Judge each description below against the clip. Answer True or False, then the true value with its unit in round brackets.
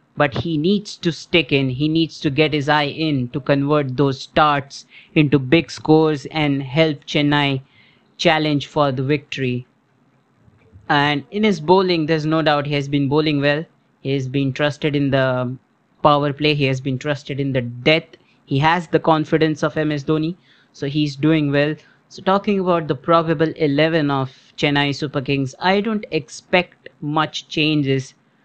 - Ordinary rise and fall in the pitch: False (2.3 semitones)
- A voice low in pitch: False (150 Hz)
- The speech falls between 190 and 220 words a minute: False (170 wpm)